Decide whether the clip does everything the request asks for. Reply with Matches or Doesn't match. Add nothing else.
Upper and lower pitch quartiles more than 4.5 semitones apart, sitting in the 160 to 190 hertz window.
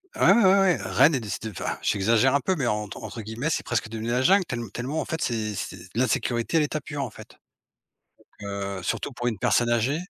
Doesn't match